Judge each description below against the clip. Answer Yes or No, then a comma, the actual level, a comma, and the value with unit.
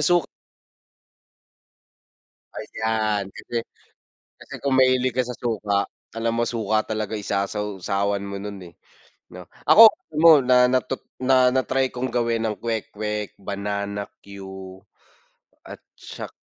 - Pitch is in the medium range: No, low, 110 Hz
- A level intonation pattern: No, average, 3.9 semitones